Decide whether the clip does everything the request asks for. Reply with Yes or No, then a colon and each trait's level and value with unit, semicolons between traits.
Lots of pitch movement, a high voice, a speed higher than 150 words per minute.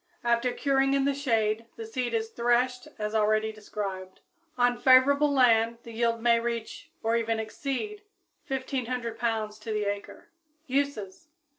No: average, 2.9 semitones; high, 235 Hz; average, 160 wpm